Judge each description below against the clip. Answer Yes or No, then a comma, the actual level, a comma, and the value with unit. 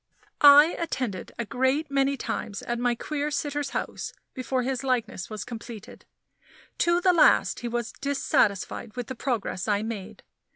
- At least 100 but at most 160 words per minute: Yes, average, 155 wpm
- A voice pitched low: No, very high, 250 Hz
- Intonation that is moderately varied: Yes, average, 3.7 semitones